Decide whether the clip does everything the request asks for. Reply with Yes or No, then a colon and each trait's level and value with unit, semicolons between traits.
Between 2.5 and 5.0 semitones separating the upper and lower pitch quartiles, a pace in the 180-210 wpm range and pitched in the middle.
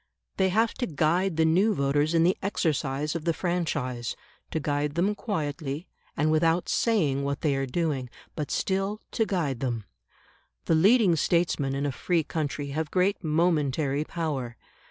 No: average, 4.1 semitones; average, 160 wpm; medium, 155 Hz